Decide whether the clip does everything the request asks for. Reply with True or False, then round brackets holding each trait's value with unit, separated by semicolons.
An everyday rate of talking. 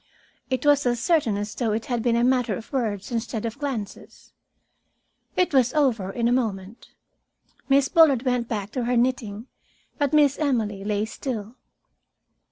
True (165 wpm)